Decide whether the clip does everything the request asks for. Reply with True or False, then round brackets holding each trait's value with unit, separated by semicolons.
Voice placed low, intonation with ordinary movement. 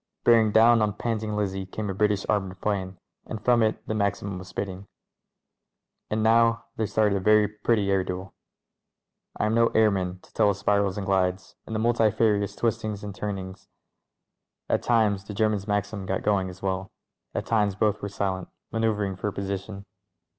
False (105 Hz; 2.1 semitones)